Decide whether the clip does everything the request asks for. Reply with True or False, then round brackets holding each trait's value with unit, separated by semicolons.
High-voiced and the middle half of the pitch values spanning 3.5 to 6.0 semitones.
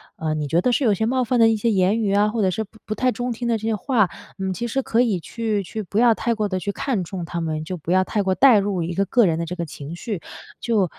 True (205 Hz; 4.1 semitones)